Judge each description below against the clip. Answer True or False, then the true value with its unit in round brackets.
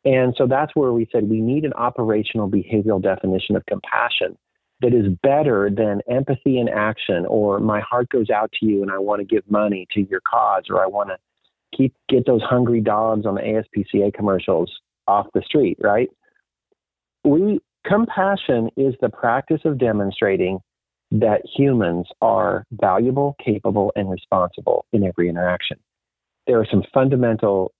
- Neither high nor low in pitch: False (110 Hz)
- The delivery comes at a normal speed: True (160 wpm)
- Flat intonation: False (4.1 semitones)